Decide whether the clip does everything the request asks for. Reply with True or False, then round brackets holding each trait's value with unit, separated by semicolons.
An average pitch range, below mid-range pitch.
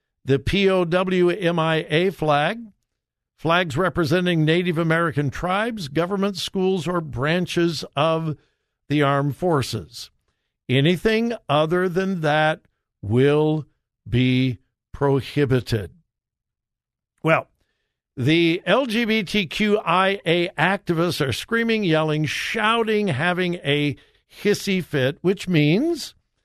False (4.5 semitones; 170 Hz)